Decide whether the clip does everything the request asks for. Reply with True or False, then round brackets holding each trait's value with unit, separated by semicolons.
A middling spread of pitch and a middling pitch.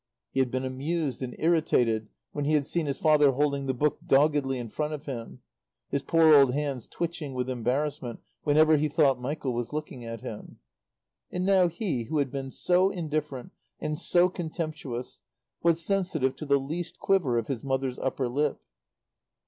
True (3.3 semitones; 145 Hz)